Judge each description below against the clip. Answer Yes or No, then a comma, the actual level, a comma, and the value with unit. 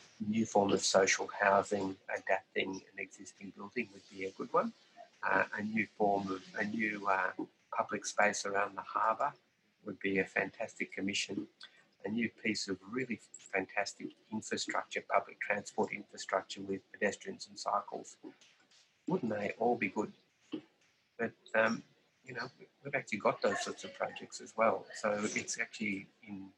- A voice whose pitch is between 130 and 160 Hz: No, low, 100 Hz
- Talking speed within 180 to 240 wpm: No, average, 155 wpm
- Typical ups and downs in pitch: No, narrow, 2.2 semitones